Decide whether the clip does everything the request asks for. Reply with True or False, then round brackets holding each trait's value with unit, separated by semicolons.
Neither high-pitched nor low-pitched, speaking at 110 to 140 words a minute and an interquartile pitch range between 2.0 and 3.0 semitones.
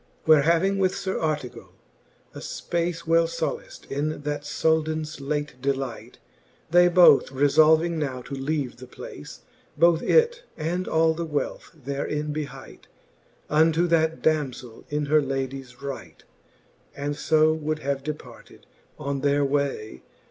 True (150 Hz; 135 wpm; 2.6 semitones)